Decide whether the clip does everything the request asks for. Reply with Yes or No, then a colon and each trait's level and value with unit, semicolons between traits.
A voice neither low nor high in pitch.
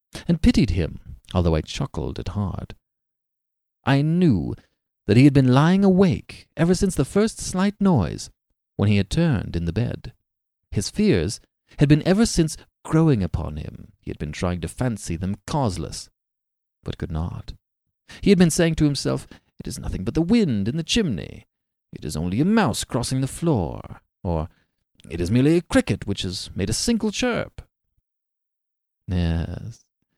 No: low, 120 Hz